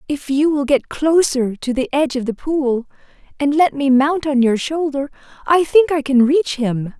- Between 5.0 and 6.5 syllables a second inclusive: No, 4.6 syllables/s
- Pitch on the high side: Yes, very high, 280 Hz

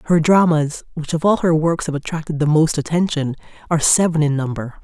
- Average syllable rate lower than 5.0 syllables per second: No, 5.8 syllables/s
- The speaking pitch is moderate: Yes, medium, 160 Hz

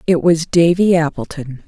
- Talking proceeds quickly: No, average, 145 wpm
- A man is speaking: No, female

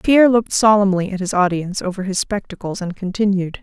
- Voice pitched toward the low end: No, high, 195 Hz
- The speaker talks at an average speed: Yes, average, 180 wpm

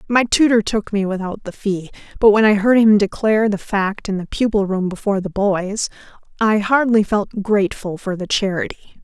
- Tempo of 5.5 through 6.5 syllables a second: No, 5.3 syllables/s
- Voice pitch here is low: No, high, 205 Hz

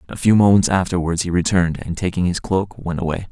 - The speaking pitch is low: Yes, very low, 90 Hz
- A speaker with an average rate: No, fast, 215 wpm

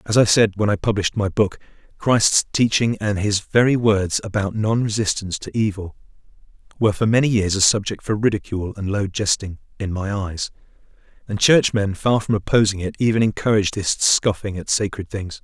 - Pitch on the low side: Yes, low, 105 Hz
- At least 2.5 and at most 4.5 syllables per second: No, 5.5 syllables/s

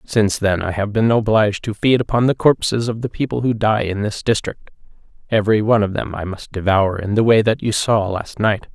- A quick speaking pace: Yes, fast, 235 wpm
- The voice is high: No, low, 105 Hz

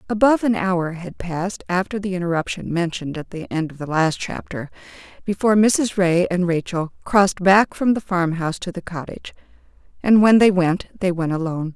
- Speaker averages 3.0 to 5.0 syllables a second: No, 5.5 syllables/s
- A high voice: No, medium, 180 Hz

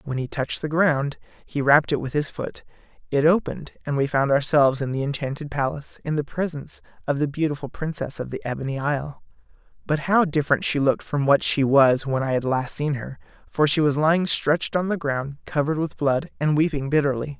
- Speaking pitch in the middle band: Yes, medium, 145 Hz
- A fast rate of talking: Yes, fast, 210 wpm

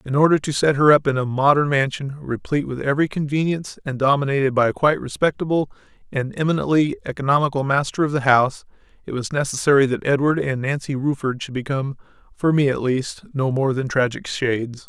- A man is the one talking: Yes, male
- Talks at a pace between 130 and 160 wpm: No, average, 185 wpm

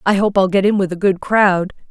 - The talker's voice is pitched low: No, high, 195 Hz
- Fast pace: Yes, fast, 285 wpm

